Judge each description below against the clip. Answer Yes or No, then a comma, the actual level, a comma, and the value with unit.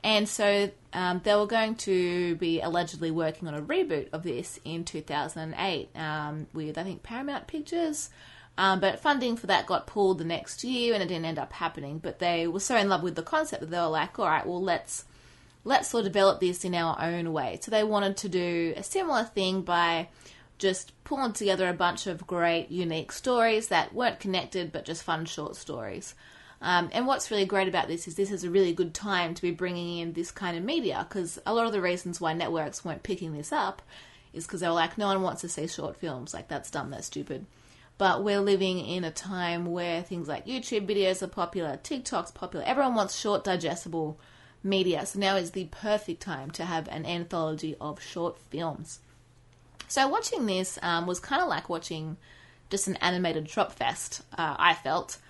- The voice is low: No, medium, 180 Hz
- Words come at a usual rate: No, fast, 210 wpm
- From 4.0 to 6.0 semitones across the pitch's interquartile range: No, average, 3.3 semitones